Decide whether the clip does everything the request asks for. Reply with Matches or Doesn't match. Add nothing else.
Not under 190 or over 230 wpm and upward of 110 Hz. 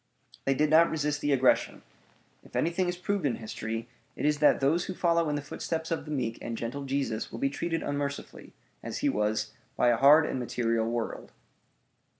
Matches